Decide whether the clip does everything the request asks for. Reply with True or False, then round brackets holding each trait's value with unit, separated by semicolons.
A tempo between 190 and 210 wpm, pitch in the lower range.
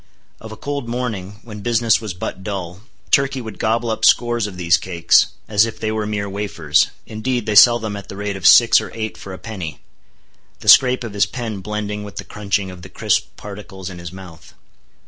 True (205 wpm; 105 Hz)